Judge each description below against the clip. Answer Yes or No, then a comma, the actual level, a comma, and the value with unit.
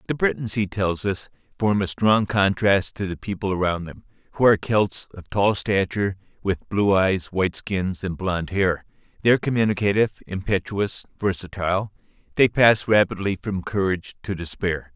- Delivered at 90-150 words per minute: No, average, 160 wpm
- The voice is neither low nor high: No, low, 100 Hz